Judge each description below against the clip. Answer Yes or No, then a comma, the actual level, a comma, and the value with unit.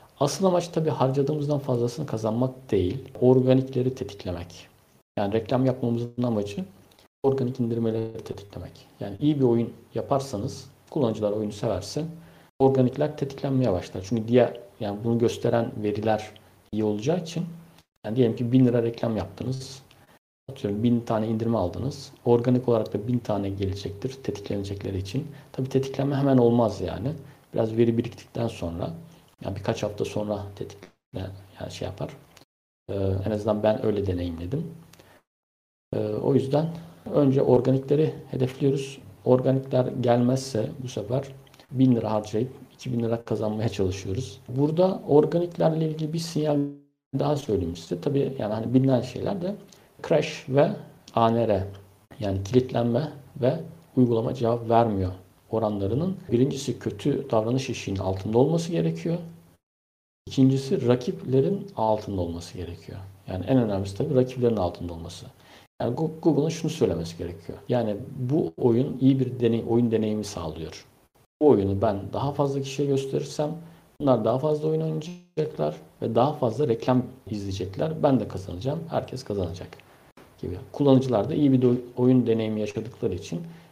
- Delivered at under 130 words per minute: No, average, 135 wpm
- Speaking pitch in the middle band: No, low, 125 Hz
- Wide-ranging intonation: No, average, 4.5 semitones